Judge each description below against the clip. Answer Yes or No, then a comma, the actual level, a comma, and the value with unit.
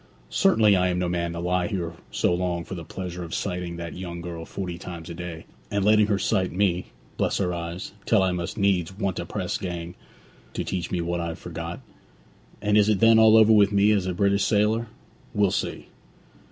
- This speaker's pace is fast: Yes, fast, 210 wpm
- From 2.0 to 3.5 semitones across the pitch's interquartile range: Yes, average, 2.9 semitones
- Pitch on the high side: No, very low, 90 Hz